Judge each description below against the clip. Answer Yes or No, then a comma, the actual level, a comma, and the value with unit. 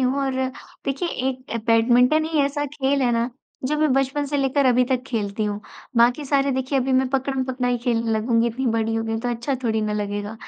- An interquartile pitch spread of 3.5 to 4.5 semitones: No, average, 3.0 semitones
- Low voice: No, very high, 255 Hz